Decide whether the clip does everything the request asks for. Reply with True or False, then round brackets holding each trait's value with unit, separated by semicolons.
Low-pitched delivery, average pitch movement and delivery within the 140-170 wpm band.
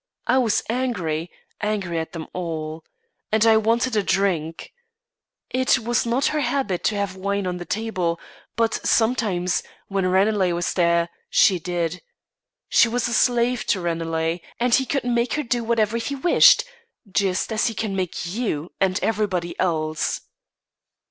False (200 Hz; 5.0 semitones; 155 wpm)